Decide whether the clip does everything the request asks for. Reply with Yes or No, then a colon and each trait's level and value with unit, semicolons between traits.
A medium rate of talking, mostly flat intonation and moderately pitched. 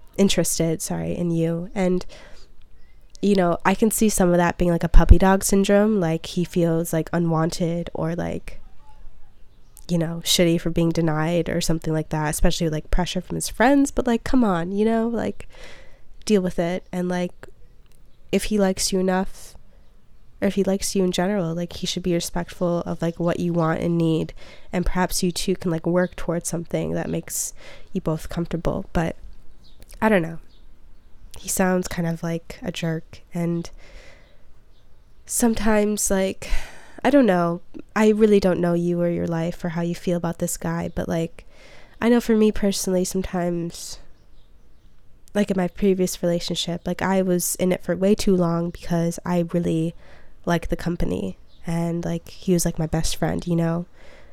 Yes: average, 180 wpm; narrow, 2.3 semitones; medium, 175 Hz